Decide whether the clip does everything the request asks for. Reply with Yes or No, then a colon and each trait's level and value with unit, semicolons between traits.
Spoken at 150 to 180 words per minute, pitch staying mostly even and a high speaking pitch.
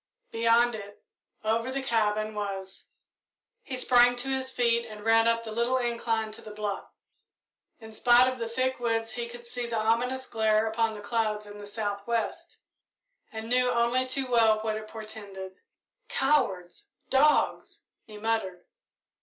Yes: average, 160 wpm; narrow, 2.2 semitones; high, 225 Hz